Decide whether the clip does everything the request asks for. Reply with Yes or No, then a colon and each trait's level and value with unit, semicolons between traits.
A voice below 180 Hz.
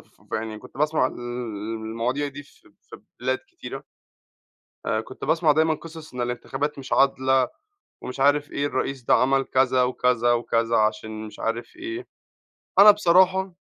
Yes: low, 135 Hz